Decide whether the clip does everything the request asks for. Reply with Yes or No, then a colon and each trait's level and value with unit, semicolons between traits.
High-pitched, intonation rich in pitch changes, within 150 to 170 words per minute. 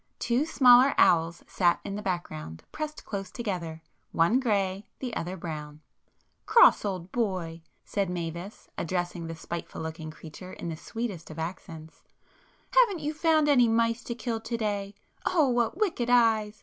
Yes: high, 200 Hz; wide, 6.2 semitones; average, 155 wpm